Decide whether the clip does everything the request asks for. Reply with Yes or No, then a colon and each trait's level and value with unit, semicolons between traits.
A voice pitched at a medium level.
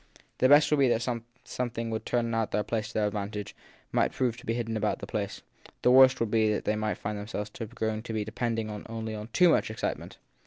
No: low, 110 Hz